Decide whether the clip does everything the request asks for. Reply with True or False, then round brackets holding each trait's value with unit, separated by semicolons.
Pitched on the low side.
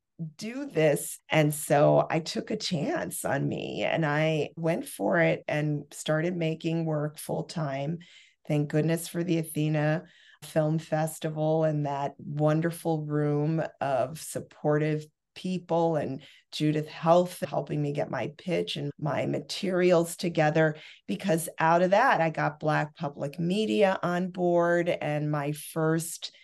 False (160 Hz)